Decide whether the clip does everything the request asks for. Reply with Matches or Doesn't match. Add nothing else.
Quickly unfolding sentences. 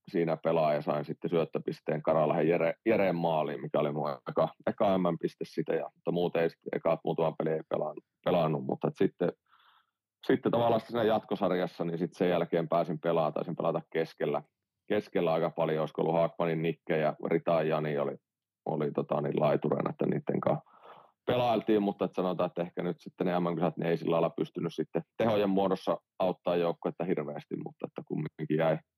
Matches